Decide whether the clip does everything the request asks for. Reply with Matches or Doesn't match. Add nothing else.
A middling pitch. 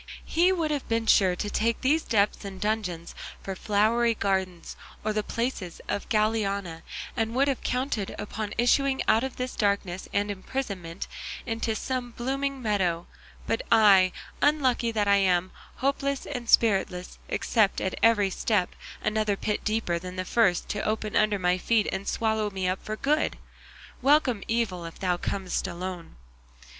Doesn't match